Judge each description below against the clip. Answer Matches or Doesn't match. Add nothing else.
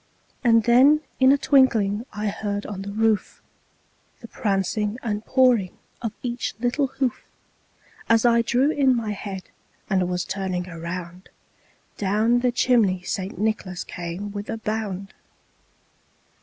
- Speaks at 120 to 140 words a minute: Matches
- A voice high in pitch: Matches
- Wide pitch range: Doesn't match